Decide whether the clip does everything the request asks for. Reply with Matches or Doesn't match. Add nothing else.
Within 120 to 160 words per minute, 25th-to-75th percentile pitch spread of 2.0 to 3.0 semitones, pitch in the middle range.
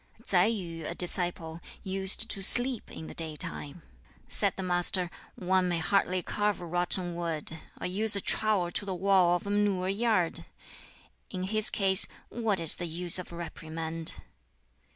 Matches